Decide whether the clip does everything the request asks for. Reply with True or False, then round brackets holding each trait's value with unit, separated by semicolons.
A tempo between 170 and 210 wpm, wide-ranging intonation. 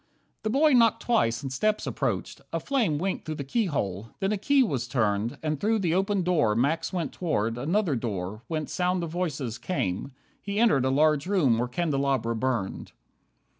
True (180 wpm; 8.0 semitones)